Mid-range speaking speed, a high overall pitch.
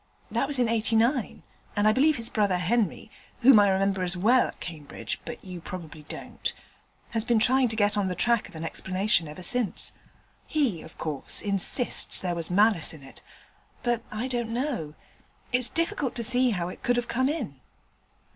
Yes: average, 185 wpm; high, 215 Hz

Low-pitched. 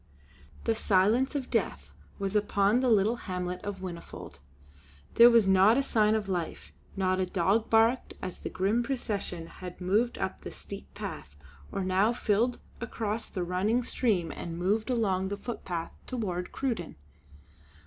No: high, 200 Hz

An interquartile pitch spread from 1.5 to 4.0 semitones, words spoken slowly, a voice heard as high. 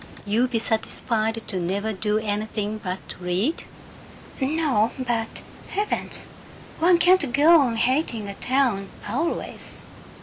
No: average, 4.9 semitones; slow, 115 wpm; high, 225 Hz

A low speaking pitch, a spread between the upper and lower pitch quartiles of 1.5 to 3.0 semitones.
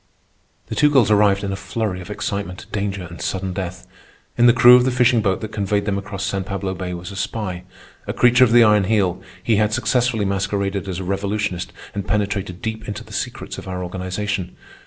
Yes: low, 100 Hz; narrow, 2.6 semitones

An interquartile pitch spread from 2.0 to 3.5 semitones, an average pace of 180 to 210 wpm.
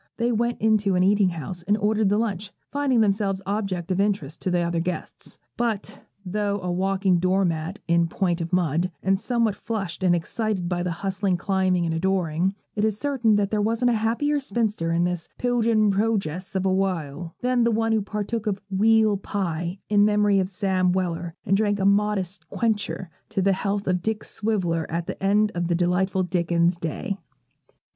Yes: average, 3.1 semitones; average, 185 wpm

